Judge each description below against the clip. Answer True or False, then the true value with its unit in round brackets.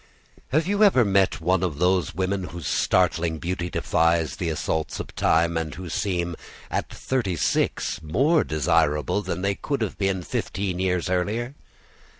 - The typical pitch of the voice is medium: False (90 Hz)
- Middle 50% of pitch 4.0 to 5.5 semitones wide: False (3.2 semitones)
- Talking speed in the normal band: True (155 wpm)